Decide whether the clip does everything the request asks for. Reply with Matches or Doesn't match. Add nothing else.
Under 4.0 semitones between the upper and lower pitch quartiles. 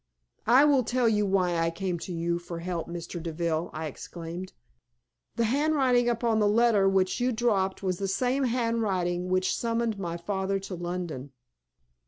Doesn't match